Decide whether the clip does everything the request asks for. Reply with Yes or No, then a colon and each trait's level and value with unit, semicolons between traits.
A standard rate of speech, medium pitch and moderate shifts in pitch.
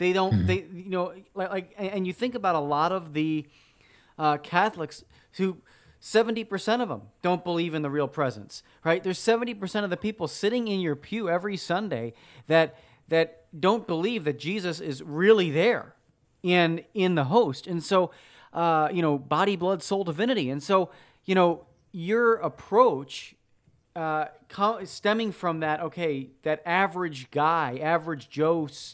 Yes: average, 160 wpm; medium, 175 Hz; average, 4.0 semitones